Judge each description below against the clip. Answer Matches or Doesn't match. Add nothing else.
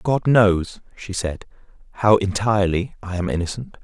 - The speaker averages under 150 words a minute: Matches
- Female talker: Doesn't match